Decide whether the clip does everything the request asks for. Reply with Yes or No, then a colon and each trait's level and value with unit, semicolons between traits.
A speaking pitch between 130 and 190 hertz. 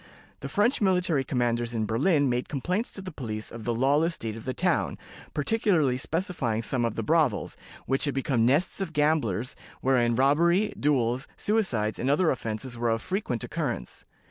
Yes: low, 135 Hz